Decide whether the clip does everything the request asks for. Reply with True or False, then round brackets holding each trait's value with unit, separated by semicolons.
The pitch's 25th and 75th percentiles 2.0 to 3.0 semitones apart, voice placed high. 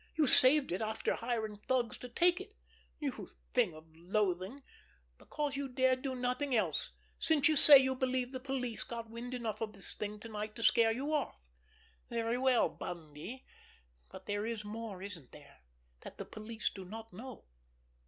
False (3.9 semitones; 230 Hz)